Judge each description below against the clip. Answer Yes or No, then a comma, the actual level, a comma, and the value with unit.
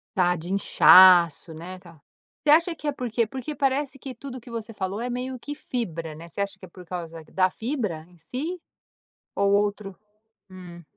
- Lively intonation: Yes, wide, 6.4 semitones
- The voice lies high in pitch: Yes, high, 200 Hz